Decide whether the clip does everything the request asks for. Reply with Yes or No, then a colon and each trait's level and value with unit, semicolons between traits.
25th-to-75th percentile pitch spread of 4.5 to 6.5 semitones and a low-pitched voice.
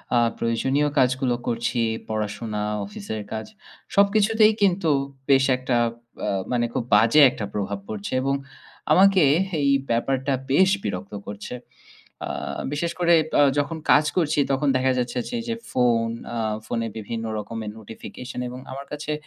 Yes: average, 4.9 semitones; low, 125 Hz